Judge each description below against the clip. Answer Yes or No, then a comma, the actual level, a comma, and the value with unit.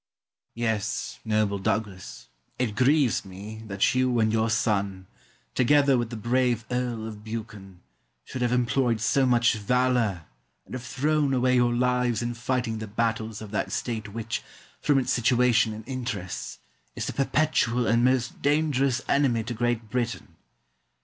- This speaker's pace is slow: No, average, 150 wpm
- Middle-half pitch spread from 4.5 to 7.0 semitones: No, narrow, 2.6 semitones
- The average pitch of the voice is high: No, low, 120 Hz